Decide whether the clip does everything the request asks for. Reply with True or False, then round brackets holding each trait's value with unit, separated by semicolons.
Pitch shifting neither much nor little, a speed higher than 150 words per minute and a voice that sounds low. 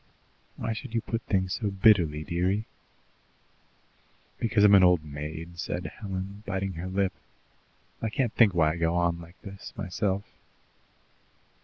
False (3.2 semitones; 145 wpm; 95 Hz)